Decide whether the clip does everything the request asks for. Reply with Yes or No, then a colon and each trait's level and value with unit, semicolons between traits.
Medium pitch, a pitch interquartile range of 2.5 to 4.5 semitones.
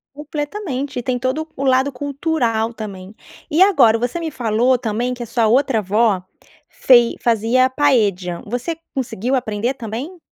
No: very high, 250 Hz; average, 3.8 semitones